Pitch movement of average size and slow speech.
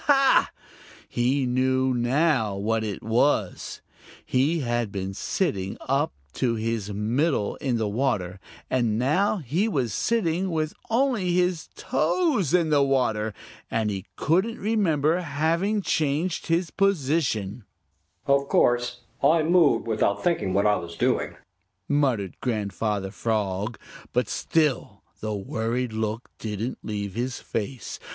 No: wide, 7.1 semitones; slow, 125 wpm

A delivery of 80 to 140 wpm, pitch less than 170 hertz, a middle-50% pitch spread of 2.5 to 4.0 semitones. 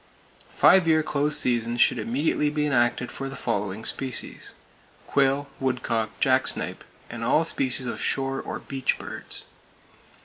Yes: slow, 135 wpm; low, 135 Hz; average, 2.9 semitones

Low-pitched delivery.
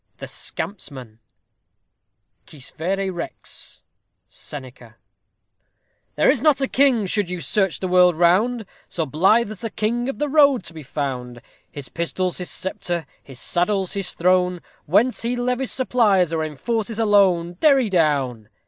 No: medium, 185 Hz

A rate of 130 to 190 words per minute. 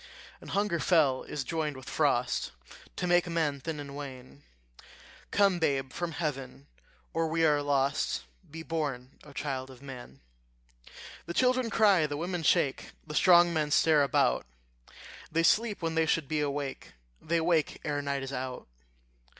Yes: average, 160 wpm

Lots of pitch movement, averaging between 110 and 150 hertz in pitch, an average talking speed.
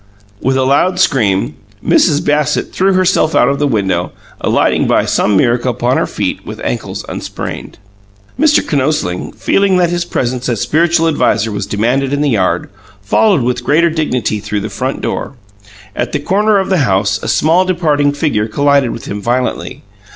Yes: wide, 6.1 semitones; medium, 140 Hz; average, 175 wpm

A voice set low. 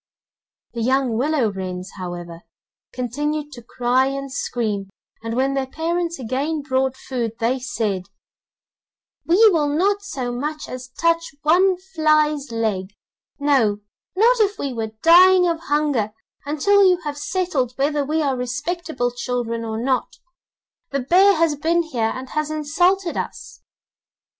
No: very high, 280 Hz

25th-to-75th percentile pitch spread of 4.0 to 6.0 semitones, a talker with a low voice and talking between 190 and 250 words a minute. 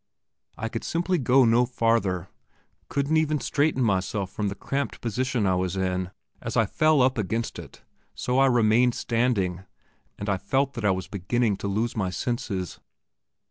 No: average, 4.8 semitones; low, 115 Hz; average, 170 wpm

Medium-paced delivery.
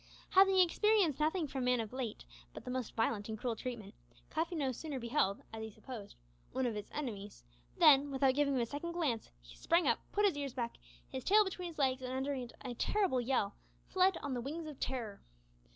No: fast, 210 wpm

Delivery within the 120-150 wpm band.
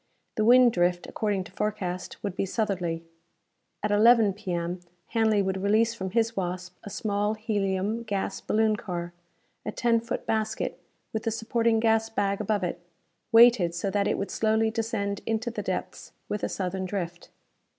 No: average, 165 wpm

